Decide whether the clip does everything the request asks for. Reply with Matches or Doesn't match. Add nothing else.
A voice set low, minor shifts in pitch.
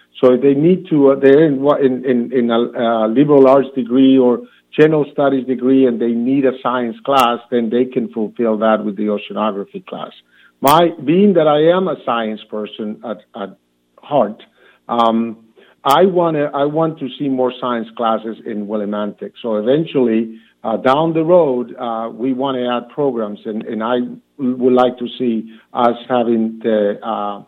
Doesn't match